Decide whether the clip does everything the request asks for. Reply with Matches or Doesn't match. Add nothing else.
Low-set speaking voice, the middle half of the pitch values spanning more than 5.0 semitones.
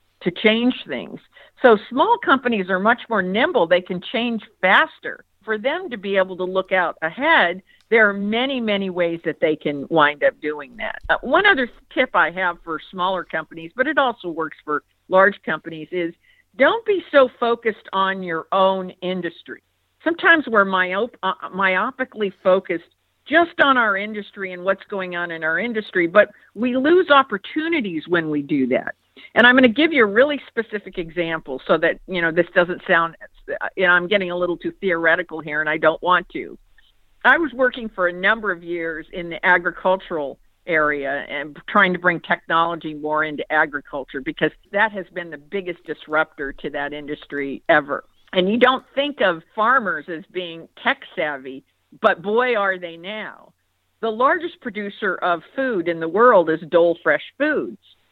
Doesn't match